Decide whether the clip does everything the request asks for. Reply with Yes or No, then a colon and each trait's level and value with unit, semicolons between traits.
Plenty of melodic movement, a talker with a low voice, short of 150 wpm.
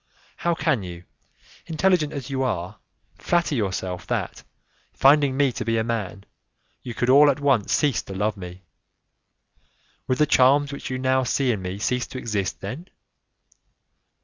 No: wide, 5.9 semitones; low, 130 Hz; average, 160 wpm